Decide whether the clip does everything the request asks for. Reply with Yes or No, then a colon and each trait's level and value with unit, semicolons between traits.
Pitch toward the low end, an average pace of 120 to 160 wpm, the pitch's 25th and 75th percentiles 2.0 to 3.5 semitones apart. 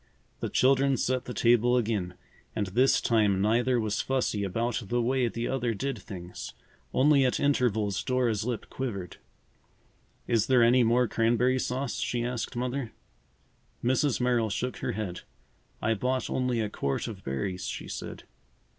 Yes: low, 120 Hz; average, 155 wpm; average, 2.9 semitones